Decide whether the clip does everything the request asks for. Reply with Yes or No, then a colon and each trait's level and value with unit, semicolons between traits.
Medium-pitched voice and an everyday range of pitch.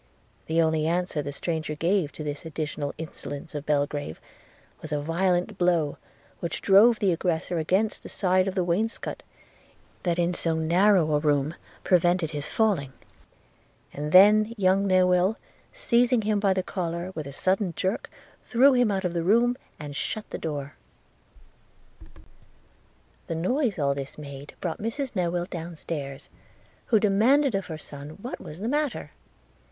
Yes: medium, 175 Hz; average, 4.8 semitones